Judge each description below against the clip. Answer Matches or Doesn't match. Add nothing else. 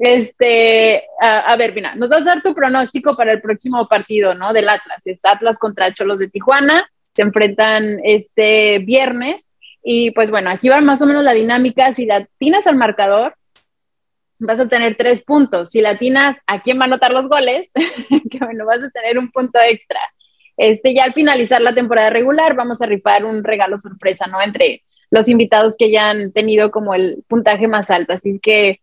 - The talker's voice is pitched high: Matches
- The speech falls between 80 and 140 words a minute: Doesn't match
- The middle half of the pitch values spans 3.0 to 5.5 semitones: Matches